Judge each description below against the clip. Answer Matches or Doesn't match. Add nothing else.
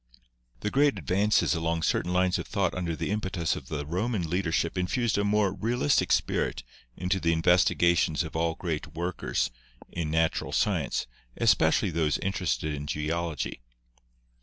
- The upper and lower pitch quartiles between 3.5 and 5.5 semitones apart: Doesn't match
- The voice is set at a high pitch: Doesn't match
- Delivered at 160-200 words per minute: Doesn't match